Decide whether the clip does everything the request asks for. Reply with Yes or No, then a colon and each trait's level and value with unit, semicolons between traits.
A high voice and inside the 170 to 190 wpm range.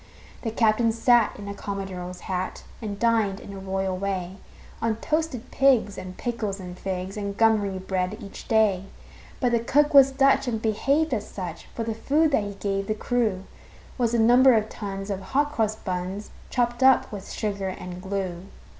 Yes: high, 210 Hz; average, 180 wpm